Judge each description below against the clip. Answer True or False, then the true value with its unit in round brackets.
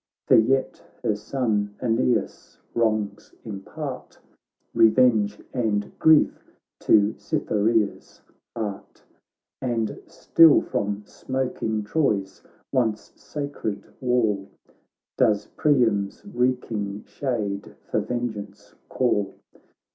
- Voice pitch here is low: True (110 Hz)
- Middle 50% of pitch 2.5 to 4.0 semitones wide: True (3.5 semitones)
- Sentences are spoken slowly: True (80 wpm)